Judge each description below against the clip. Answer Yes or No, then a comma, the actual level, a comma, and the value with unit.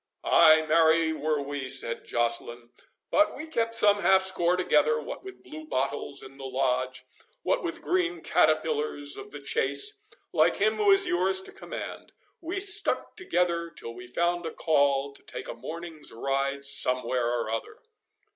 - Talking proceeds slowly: No, average, 165 wpm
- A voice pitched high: No, medium, 160 Hz